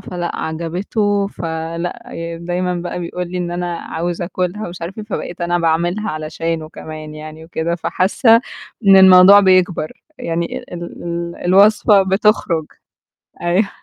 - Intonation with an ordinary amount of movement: No, narrow, 2.2 semitones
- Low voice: No, medium, 175 Hz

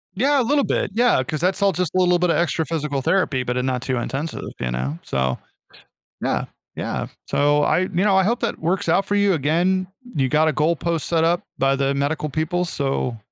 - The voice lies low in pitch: No, medium, 160 Hz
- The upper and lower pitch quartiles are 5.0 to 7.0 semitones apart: Yes, average, 5.3 semitones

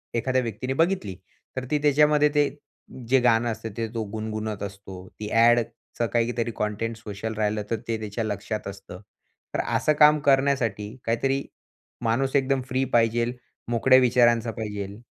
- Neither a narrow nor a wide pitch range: Yes, average, 3.3 semitones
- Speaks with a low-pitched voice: Yes, low, 115 Hz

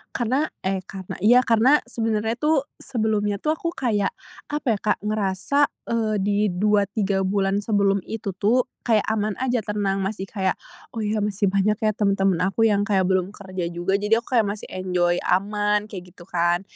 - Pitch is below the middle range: No, high, 205 Hz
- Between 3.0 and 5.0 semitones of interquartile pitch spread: No, narrow, 2.4 semitones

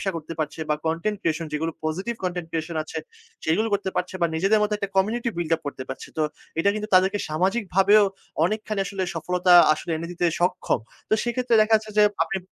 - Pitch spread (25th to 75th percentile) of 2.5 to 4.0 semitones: No, average, 4.4 semitones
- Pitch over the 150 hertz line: Yes, medium, 185 Hz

